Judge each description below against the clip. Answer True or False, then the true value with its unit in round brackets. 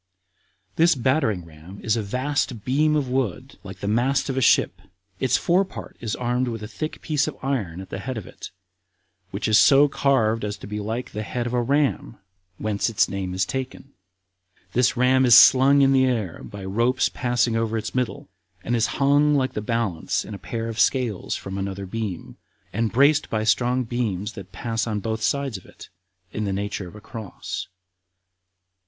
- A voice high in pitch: False (115 Hz)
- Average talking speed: True (195 wpm)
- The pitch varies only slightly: False (4.1 semitones)